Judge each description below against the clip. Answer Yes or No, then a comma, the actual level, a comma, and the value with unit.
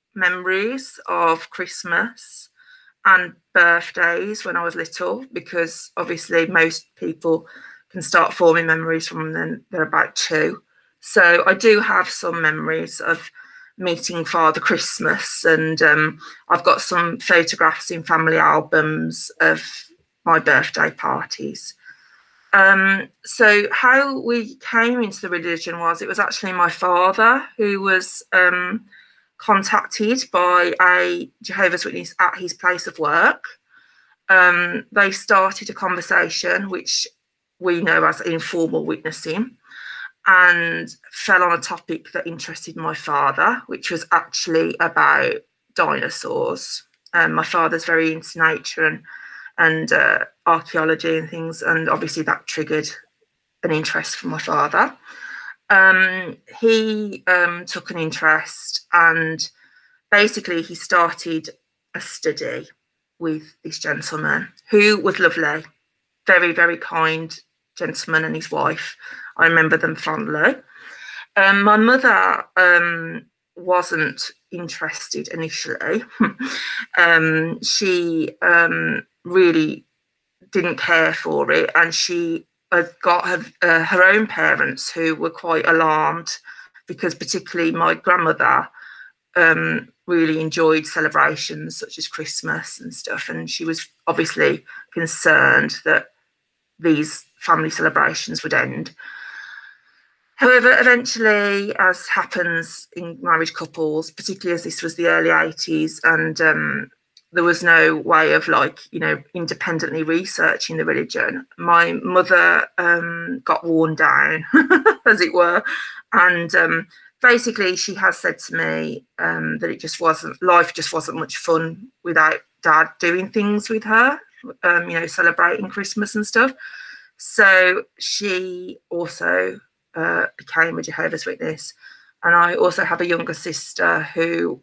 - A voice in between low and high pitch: Yes, medium, 180 Hz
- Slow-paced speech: Yes, slow, 125 wpm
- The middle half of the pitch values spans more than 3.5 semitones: Yes, average, 5.2 semitones